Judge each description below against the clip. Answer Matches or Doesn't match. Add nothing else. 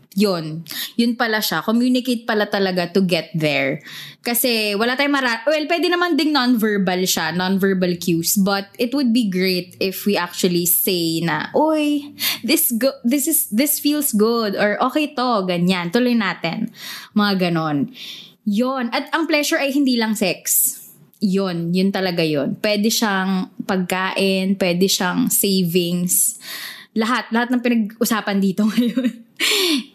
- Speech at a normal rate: Matches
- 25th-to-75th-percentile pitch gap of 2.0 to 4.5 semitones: Doesn't match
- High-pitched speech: Matches